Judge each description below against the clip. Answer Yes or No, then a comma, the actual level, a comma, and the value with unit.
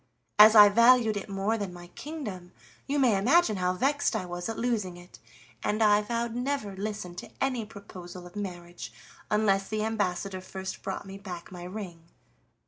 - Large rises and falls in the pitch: No, average, 3.6 semitones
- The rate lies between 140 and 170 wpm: No, average, 180 wpm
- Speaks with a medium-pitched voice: No, high, 205 Hz